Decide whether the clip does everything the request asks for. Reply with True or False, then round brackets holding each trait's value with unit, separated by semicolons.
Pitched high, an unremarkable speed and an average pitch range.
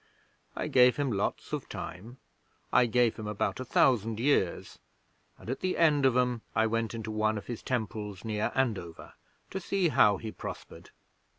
False (115 Hz; 175 wpm; 3.1 semitones)